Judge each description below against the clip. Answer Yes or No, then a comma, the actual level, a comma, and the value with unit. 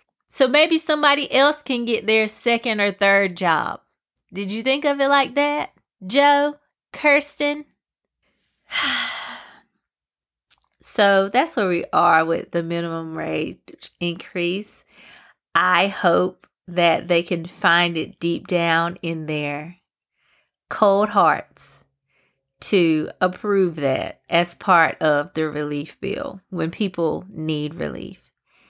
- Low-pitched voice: No, medium, 185 Hz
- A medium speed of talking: No, slow, 115 wpm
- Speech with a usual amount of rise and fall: No, wide, 6.2 semitones